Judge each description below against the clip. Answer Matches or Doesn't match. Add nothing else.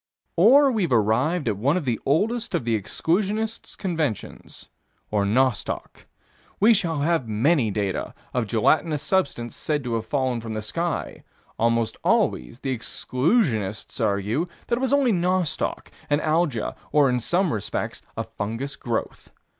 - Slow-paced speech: Doesn't match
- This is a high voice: Doesn't match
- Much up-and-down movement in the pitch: Matches